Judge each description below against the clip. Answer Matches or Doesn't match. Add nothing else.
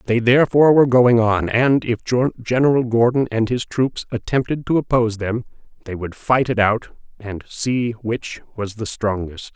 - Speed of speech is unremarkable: Matches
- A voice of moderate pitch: Doesn't match